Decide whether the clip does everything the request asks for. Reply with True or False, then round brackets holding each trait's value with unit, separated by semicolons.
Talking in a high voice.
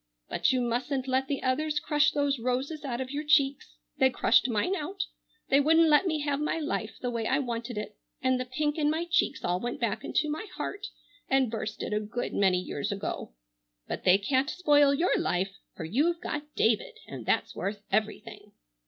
True (265 Hz)